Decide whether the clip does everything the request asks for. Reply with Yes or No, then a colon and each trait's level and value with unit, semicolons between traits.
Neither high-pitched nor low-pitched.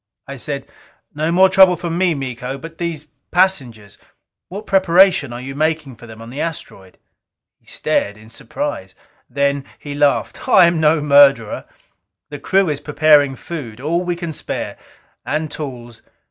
Yes: medium, 145 Hz